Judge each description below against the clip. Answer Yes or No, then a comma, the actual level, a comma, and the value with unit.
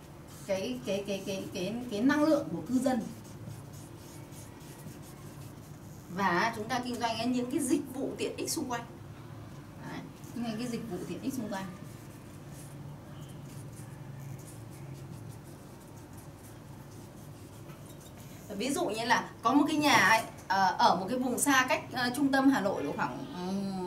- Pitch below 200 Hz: Yes, medium, 185 Hz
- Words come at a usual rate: No, slow, 145 wpm